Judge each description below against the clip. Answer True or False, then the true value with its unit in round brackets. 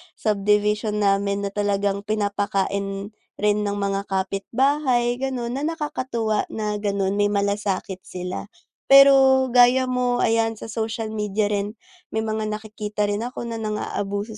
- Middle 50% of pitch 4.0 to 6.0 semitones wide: False (2.7 semitones)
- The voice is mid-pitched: False (210 Hz)